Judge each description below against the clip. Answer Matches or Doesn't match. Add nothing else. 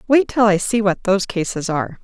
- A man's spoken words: Doesn't match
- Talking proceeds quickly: Matches